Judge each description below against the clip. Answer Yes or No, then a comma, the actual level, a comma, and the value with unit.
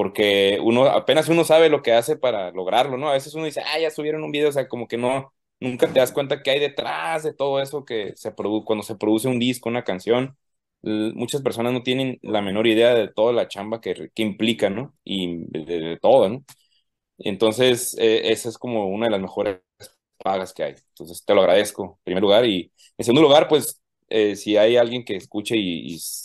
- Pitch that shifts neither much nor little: Yes, average, 4.1 semitones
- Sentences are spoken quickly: Yes, fast, 220 wpm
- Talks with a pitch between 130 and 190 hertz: No, low, 120 Hz